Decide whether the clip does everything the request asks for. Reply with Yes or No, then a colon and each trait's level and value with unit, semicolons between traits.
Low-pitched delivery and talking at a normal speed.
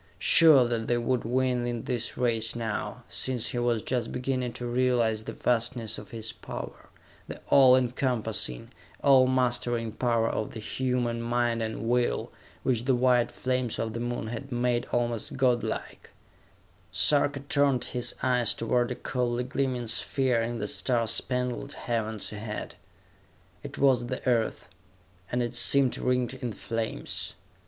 Yes: low, 120 Hz; average, 150 wpm